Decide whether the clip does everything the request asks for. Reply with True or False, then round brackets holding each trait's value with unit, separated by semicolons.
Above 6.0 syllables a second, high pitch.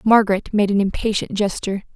True (6.3 syllables/s; 205 Hz)